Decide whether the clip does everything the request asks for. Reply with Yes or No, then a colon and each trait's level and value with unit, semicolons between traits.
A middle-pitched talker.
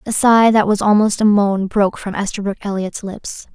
No: high, 205 Hz